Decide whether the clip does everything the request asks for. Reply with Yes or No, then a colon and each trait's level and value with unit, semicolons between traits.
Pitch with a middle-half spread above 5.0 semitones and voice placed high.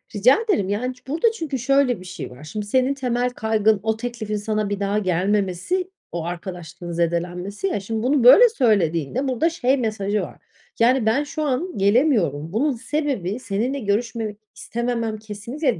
No: average, 4.7 semitones; high, 225 Hz